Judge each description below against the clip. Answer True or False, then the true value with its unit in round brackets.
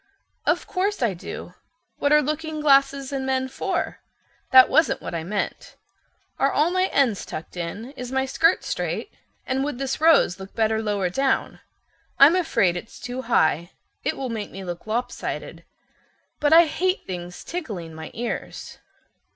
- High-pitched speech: True (260 Hz)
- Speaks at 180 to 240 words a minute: False (160 wpm)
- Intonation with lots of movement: True (7.0 semitones)